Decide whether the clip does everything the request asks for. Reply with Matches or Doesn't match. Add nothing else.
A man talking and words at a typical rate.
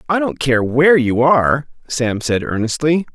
Matches